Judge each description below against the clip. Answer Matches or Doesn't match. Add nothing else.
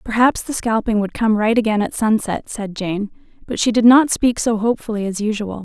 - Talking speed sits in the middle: Doesn't match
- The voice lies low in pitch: Doesn't match